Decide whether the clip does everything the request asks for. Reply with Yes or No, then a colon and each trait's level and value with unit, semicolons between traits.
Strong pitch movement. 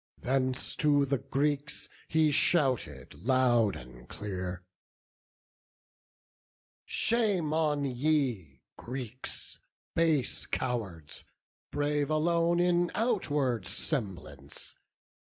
Yes: wide, 6.3 semitones